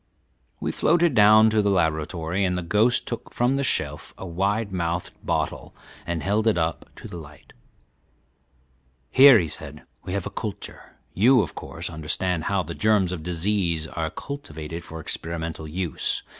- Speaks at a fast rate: No, average, 165 wpm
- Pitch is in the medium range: No, very low, 90 Hz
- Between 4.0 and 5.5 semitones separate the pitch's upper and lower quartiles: Yes, average, 4.5 semitones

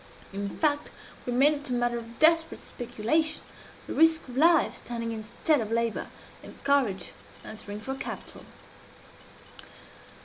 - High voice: Yes, high, 245 Hz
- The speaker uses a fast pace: No, slow, 135 wpm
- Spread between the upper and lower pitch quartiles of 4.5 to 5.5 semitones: Yes, average, 4.9 semitones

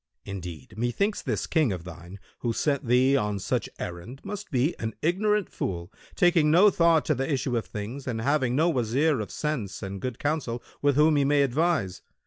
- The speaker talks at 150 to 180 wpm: No, average, 190 wpm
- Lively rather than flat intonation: Yes, wide, 6.4 semitones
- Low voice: Yes, low, 130 Hz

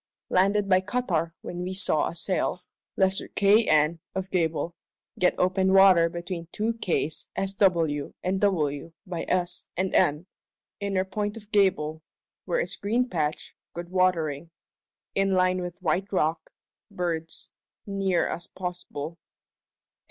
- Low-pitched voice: No, medium, 185 Hz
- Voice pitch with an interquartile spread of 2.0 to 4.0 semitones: Yes, average, 2.7 semitones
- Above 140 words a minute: No, slow, 135 wpm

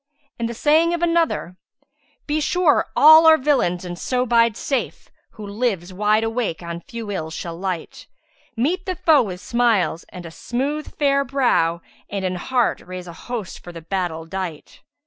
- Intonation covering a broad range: Yes, wide, 7.7 semitones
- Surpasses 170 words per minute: Yes, average, 180 wpm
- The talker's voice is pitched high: Yes, high, 225 Hz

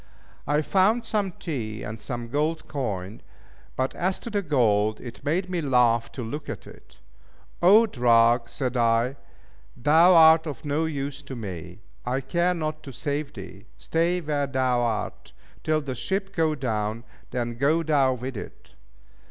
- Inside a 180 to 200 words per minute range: No, average, 160 wpm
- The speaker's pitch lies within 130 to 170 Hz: Yes, low, 135 Hz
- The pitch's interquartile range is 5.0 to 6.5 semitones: Yes, average, 5.3 semitones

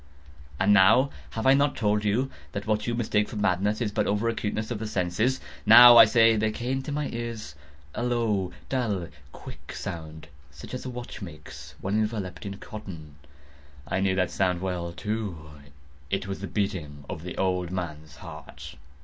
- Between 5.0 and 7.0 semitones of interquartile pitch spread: No, average, 4.2 semitones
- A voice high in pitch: No, low, 105 Hz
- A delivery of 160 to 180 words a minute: Yes, average, 175 wpm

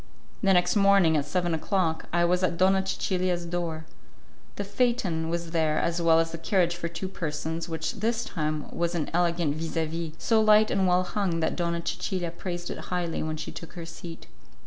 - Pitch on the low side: No, medium, 170 Hz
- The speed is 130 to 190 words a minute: No, average, 200 wpm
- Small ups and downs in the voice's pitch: Yes, narrow, 2.2 semitones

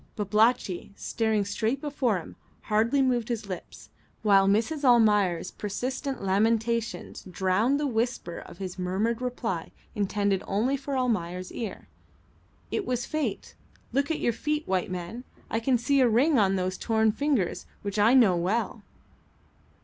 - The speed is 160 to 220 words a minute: No, average, 145 wpm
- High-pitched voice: Yes, high, 220 Hz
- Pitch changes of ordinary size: Yes, average, 4.3 semitones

